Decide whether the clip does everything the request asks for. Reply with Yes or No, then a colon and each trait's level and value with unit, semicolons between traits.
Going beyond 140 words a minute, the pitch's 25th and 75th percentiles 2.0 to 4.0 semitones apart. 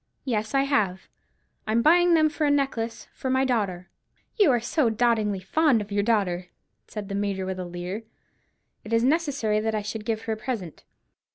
No: average, 195 wpm; average, 4.6 semitones